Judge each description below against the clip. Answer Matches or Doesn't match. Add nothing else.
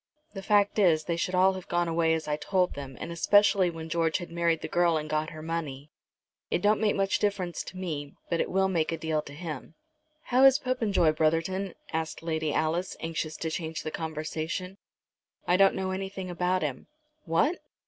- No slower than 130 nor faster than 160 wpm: Doesn't match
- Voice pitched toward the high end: Doesn't match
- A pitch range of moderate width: Matches